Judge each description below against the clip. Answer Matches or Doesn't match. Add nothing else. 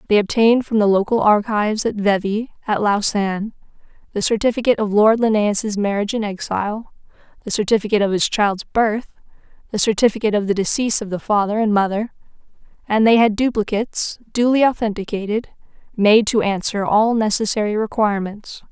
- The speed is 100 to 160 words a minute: Matches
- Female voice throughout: Matches